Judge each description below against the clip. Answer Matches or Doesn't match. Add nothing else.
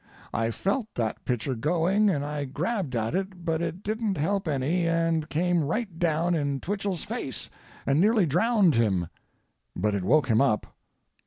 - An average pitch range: Doesn't match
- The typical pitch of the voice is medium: Matches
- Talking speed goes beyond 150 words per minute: Matches